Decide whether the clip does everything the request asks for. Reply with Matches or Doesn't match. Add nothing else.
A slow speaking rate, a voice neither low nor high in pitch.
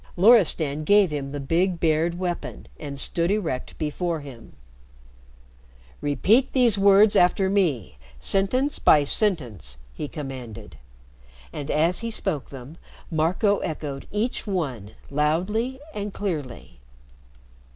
Matches